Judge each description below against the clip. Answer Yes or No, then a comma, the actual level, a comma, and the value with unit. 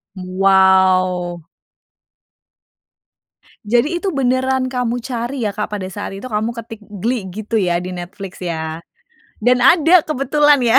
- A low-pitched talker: No, high, 215 Hz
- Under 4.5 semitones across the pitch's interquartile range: No, wide, 5.4 semitones